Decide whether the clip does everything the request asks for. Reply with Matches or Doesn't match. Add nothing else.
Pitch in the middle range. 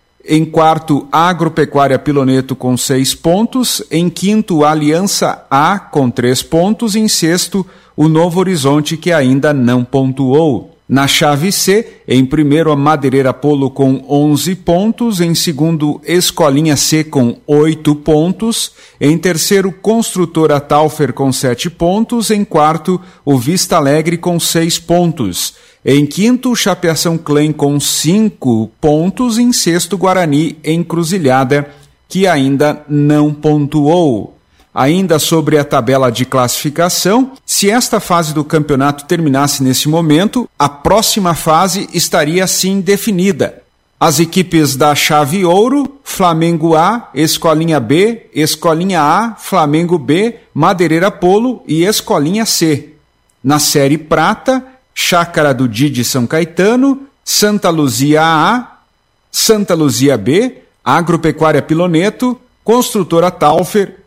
Matches